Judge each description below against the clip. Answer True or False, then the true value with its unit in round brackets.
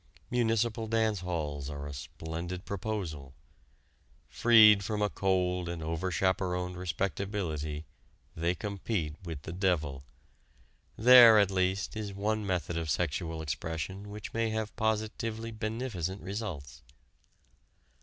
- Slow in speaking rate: True (115 wpm)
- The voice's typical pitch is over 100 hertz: False (95 Hz)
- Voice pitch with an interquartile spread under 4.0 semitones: False (4.8 semitones)